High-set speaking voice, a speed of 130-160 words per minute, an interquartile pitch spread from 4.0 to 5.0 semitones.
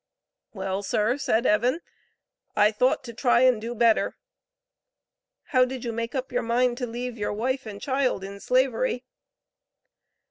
No: high, 240 Hz; average, 150 wpm; average, 2.8 semitones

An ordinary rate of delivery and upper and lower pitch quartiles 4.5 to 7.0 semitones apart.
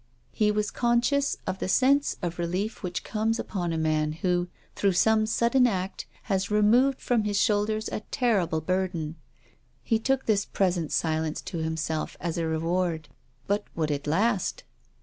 Yes: average, 160 wpm; average, 4.9 semitones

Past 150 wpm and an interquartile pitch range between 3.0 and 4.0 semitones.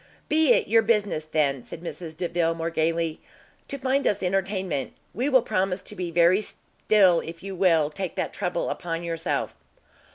Yes: average, 170 wpm; average, 3.7 semitones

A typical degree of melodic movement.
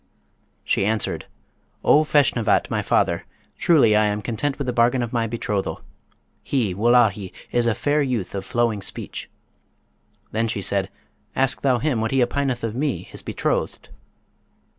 Yes: average, 3.8 semitones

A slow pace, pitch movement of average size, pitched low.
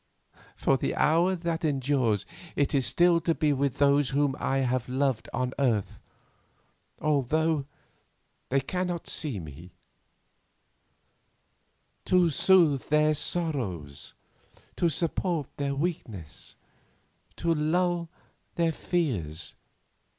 No: slow, 105 wpm; average, 4.5 semitones; medium, 145 Hz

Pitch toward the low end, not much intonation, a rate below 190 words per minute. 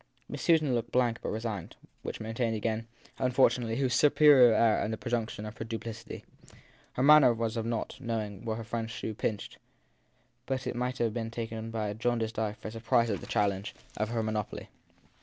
No: low, 115 Hz; narrow, 1.8 semitones; average, 195 wpm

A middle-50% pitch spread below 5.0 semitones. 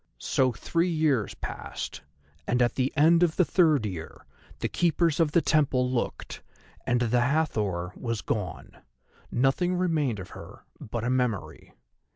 No: wide, 5.4 semitones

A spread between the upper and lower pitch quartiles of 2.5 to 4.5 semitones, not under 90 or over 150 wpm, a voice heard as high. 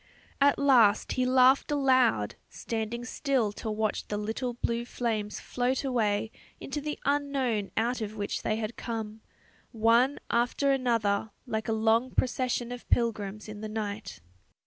Yes: average, 3.0 semitones; average, 145 wpm; high, 235 Hz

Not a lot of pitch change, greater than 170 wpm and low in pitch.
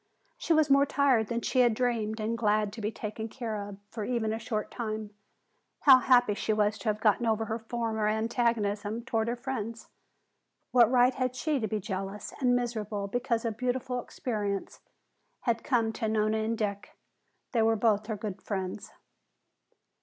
No: narrow, 2.3 semitones; average, 180 wpm; high, 225 Hz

